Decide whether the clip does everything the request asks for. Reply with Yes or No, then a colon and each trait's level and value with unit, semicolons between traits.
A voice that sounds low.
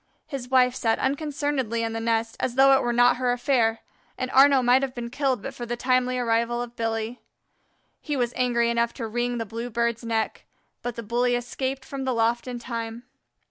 No: high, 240 Hz